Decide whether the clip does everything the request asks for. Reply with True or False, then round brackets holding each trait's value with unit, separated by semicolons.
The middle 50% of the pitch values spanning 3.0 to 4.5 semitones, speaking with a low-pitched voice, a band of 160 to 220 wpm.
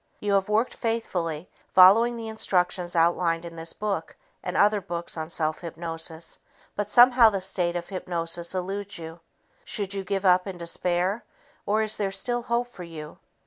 False (3.6 semitones; 185 Hz; 170 wpm)